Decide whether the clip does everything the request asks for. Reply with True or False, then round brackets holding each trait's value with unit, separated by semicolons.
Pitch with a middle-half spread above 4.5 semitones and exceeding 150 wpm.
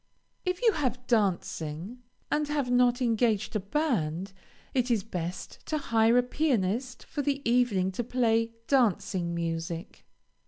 False (5.2 semitones; 135 wpm)